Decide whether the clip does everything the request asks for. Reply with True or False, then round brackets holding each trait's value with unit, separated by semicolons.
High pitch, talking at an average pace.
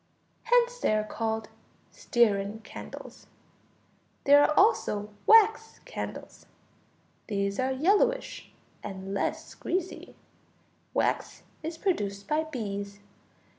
False (240 Hz; 95 wpm)